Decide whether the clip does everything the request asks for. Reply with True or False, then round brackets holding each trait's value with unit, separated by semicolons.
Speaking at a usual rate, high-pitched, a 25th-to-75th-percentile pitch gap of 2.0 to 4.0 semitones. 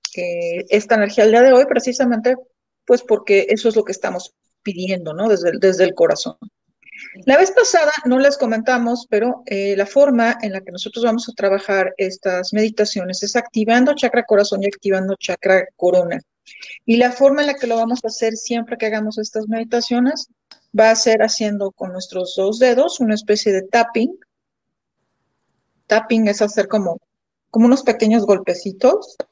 True (170 wpm; 220 Hz; 3.6 semitones)